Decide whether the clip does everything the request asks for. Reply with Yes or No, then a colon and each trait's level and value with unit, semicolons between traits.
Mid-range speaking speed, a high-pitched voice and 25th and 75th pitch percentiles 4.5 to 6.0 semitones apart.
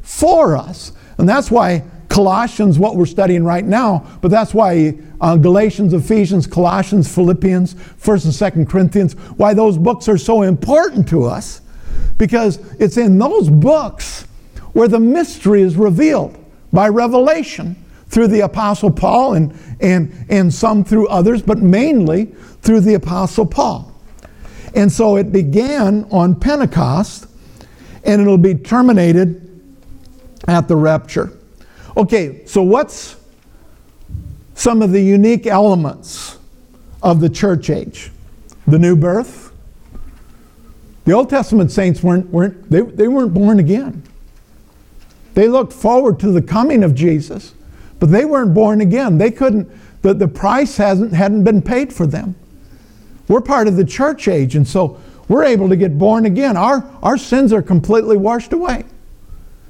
No: average, 145 wpm; high, 200 Hz; average, 3.9 semitones